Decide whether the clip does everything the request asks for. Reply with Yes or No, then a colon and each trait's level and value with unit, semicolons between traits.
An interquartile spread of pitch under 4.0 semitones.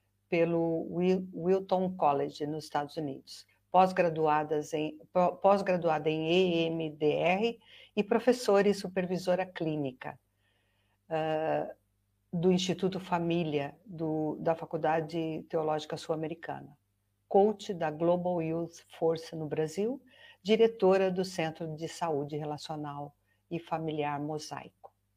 Yes: average, 3.3 semitones